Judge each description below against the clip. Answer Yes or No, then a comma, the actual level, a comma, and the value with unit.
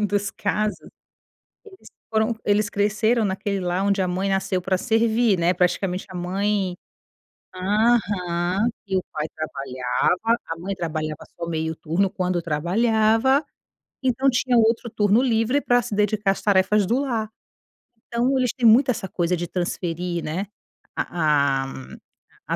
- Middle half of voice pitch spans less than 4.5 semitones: Yes, average, 4.1 semitones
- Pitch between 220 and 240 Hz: No, high, 200 Hz